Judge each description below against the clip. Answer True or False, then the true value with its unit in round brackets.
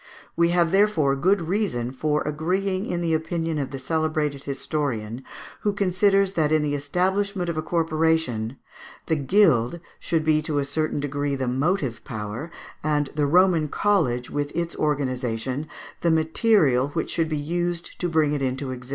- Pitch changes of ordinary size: True (3.9 semitones)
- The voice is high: False (155 Hz)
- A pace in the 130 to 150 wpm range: False (165 wpm)